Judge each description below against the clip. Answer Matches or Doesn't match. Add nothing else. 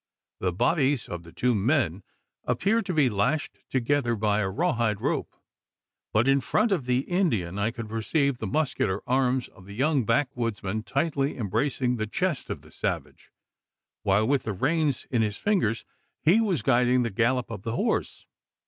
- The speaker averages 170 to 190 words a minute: Matches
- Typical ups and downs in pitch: Matches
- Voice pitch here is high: Doesn't match